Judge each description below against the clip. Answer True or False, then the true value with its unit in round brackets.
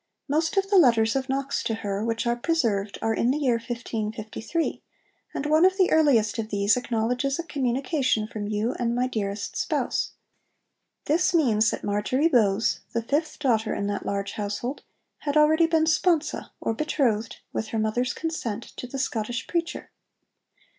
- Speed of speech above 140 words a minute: True (165 wpm)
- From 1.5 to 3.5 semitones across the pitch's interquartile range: False (5.6 semitones)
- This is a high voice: True (240 Hz)